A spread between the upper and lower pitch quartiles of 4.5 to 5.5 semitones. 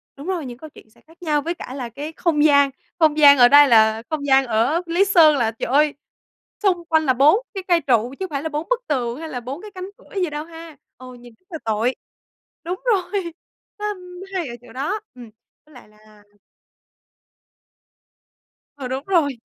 Yes: average, 5.2 semitones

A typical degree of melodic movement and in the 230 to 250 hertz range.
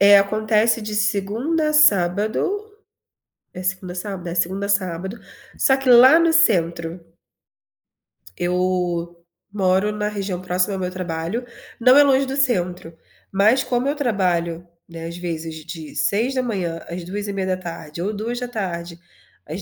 No: average, 4.6 semitones; high, 195 Hz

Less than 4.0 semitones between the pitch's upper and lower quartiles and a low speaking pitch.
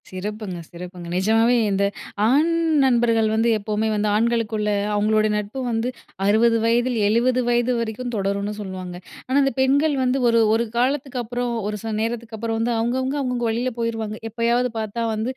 No: narrow, 2.4 semitones; high, 230 Hz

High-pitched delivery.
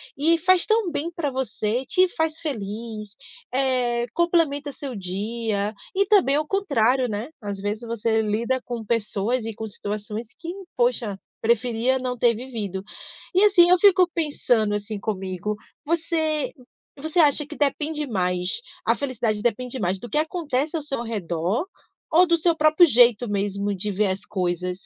Yes: high, 240 Hz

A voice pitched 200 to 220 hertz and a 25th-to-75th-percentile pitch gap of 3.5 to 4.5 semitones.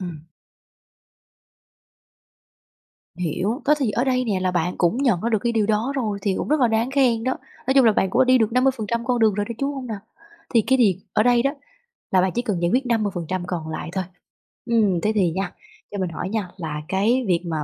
No: high, 215 Hz; average, 5.0 semitones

